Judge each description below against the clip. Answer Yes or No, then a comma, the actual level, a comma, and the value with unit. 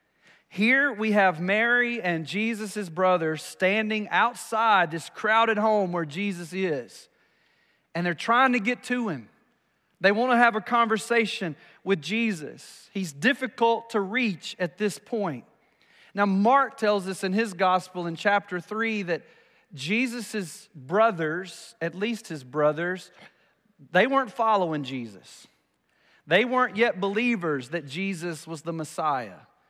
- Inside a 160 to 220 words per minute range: No, slow, 135 wpm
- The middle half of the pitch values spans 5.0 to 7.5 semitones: No, average, 4.6 semitones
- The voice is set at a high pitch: Yes, high, 205 Hz